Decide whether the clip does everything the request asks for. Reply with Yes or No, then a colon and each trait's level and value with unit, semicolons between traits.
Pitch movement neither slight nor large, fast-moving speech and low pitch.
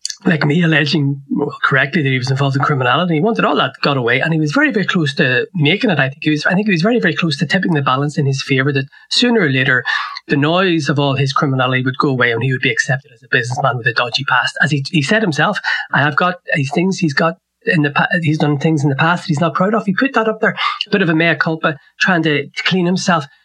No: average, 3.9 semitones; fast, 285 wpm; medium, 160 Hz